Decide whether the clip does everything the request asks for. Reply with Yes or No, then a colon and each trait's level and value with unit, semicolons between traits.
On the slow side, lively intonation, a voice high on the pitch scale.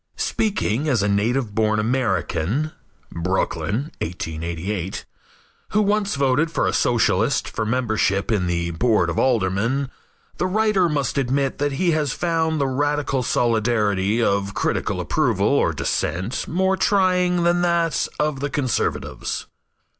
No: slow, 130 wpm; wide, 7.4 semitones; low, 130 Hz